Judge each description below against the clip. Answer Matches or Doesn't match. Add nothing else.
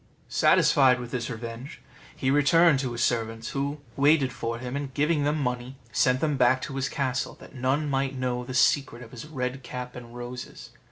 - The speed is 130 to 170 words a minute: Doesn't match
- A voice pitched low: Matches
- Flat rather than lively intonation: Matches